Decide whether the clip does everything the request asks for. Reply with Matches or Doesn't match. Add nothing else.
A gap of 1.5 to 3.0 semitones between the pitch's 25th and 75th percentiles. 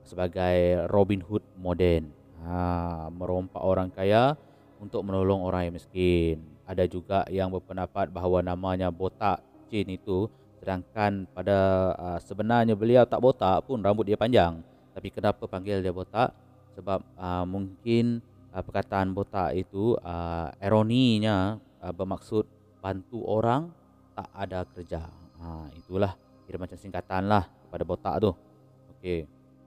Matches